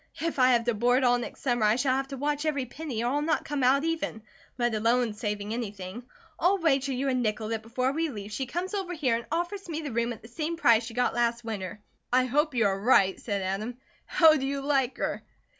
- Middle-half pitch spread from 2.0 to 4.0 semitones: No, average, 4.4 semitones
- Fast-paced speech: Yes, fast, 240 wpm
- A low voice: No, very high, 250 Hz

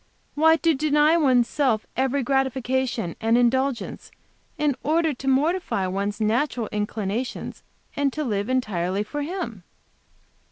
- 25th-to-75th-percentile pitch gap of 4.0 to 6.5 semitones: Yes, average, 5.2 semitones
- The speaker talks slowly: Yes, slow, 125 wpm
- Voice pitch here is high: Yes, very high, 260 Hz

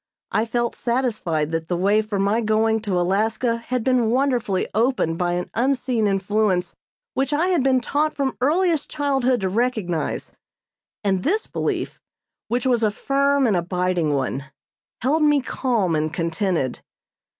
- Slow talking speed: No, average, 150 wpm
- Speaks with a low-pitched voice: No, high, 225 Hz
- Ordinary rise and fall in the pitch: No, wide, 6.0 semitones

